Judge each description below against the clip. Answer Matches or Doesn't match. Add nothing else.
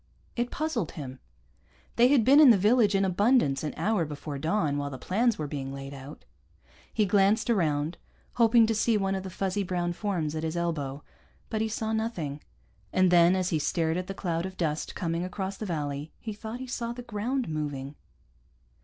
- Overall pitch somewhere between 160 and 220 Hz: Matches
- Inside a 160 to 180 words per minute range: Doesn't match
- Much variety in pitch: Matches